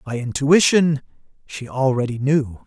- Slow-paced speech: Yes, slow, 115 wpm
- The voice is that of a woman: No, male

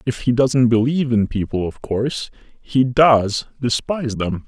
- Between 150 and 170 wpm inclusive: Yes, average, 160 wpm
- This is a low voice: Yes, low, 120 Hz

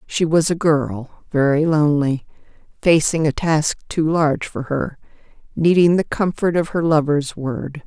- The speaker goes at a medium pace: Yes, average, 155 wpm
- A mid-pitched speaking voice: Yes, medium, 155 Hz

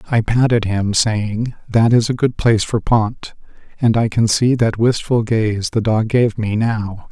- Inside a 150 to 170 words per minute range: No, average, 195 wpm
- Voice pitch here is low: Yes, low, 110 Hz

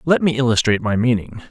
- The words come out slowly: No, average, 200 wpm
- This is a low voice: Yes, low, 130 Hz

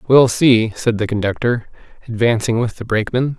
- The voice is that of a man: Yes, male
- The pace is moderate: Yes, average, 160 wpm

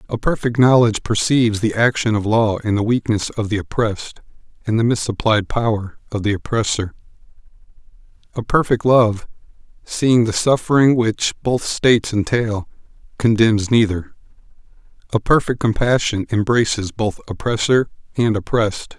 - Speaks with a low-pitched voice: Yes, low, 110 Hz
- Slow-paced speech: Yes, slow, 130 wpm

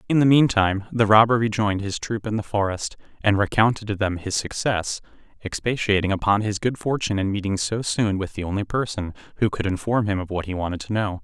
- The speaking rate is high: Yes, fast, 215 wpm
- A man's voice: Yes, male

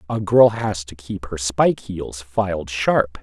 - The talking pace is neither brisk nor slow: Yes, average, 185 wpm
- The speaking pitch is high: No, very low, 95 Hz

